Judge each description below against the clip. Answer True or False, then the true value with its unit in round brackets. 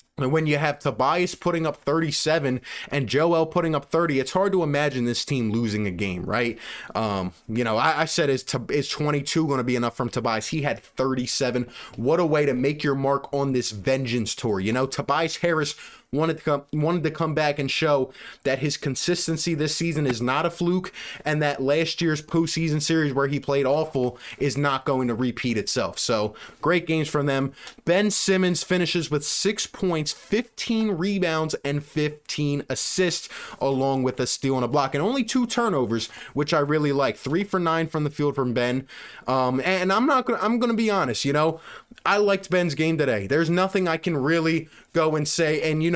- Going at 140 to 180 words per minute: False (205 wpm)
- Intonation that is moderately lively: True (4.0 semitones)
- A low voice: False (150 Hz)